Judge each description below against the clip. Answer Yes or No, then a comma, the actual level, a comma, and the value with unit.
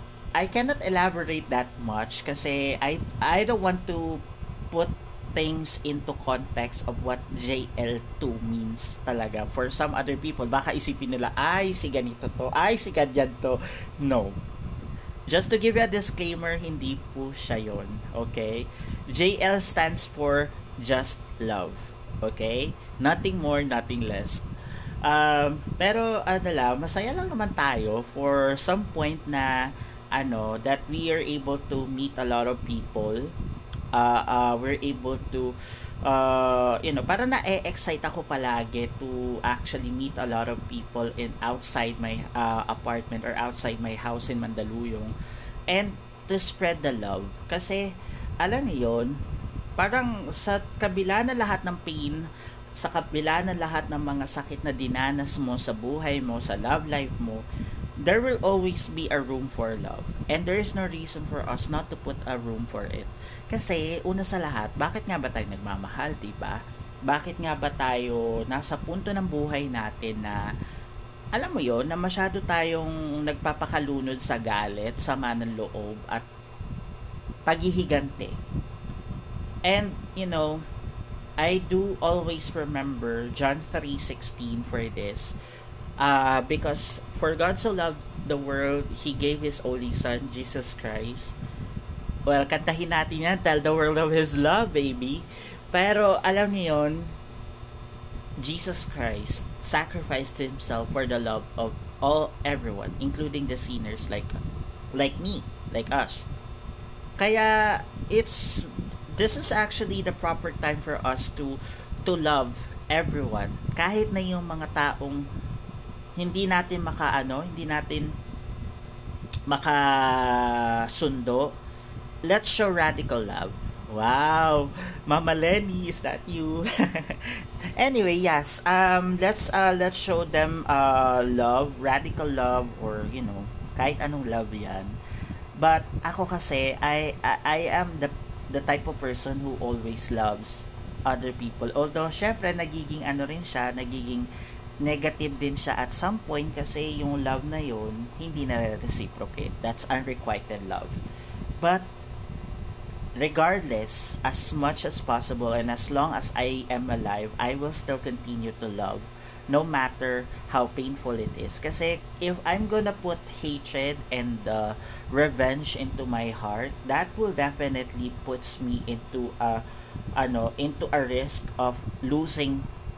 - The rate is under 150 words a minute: Yes, average, 140 wpm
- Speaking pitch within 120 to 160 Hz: Yes, low, 135 Hz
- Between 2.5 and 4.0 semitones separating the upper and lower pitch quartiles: No, average, 4.7 semitones